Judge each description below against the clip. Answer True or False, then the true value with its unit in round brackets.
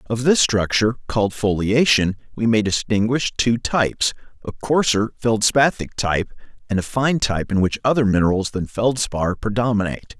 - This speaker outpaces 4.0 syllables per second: True (5.3 syllables/s)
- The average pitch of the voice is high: False (110 Hz)